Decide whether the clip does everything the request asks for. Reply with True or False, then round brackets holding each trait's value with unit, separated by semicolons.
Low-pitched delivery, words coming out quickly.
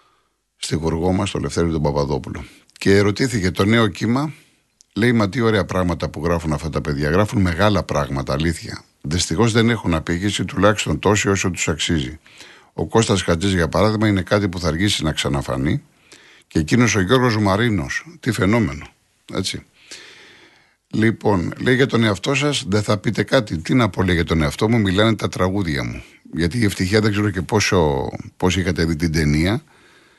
True (95 Hz; 175 wpm)